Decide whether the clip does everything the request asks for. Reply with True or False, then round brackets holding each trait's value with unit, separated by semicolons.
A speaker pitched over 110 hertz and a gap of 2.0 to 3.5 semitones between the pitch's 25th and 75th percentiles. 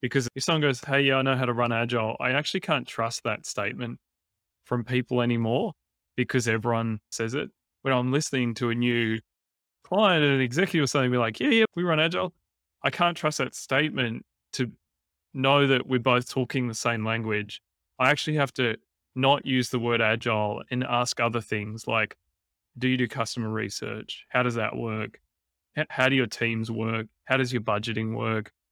True (120 Hz; 3.1 semitones)